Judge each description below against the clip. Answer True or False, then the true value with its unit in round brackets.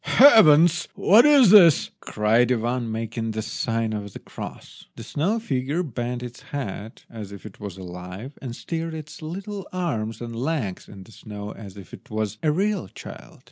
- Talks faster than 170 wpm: True (180 wpm)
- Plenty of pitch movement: True (7.2 semitones)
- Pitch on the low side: True (120 Hz)